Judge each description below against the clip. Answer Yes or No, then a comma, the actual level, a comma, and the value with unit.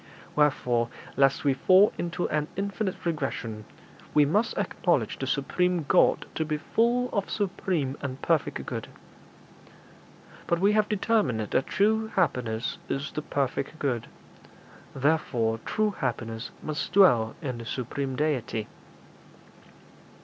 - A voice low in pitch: No, medium, 150 Hz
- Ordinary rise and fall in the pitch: No, wide, 6.9 semitones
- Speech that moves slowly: Yes, slow, 125 wpm